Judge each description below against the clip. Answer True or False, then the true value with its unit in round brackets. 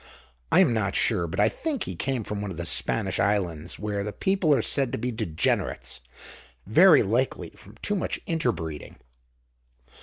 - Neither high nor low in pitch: False (110 Hz)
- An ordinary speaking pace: True (180 wpm)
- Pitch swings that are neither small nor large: False (6.2 semitones)